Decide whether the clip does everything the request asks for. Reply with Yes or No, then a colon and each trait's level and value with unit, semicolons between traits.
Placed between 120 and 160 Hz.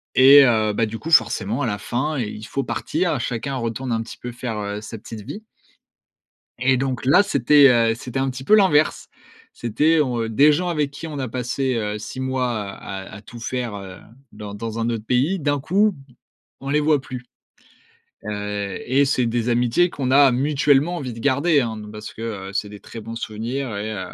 Yes: low, 125 Hz